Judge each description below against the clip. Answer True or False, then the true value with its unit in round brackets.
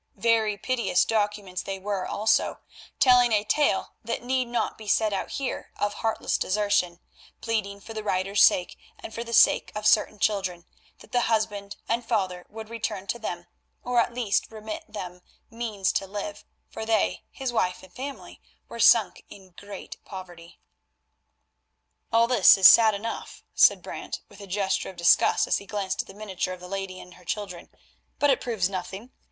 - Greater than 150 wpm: True (180 wpm)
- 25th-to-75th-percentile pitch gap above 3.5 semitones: False (3.2 semitones)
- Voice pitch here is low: False (210 Hz)